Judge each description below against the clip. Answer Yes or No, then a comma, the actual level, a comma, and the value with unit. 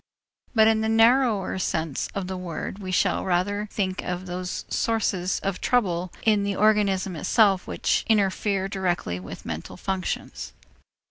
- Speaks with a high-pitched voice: Yes, high, 195 Hz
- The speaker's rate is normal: Yes, average, 150 wpm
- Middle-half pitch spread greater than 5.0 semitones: No, narrow, 2.6 semitones